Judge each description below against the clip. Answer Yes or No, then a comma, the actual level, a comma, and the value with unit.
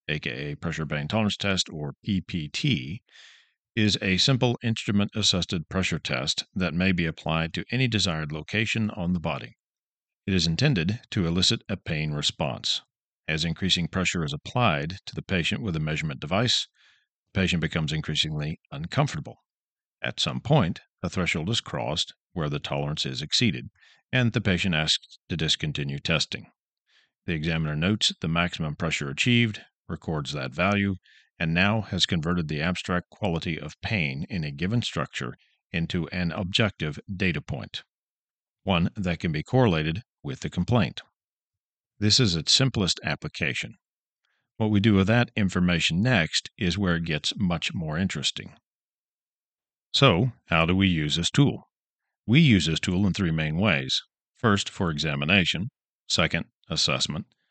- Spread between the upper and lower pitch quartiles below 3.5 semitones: No, average, 4.7 semitones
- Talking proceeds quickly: No, average, 150 wpm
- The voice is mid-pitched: No, very low, 90 Hz